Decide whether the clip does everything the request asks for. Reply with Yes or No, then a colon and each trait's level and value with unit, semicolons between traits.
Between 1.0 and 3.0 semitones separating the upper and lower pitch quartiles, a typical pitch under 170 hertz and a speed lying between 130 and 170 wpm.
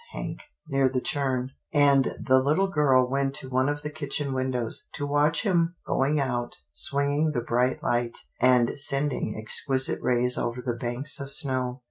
Yes: narrow, 2.4 semitones; low, 135 Hz; average, 165 wpm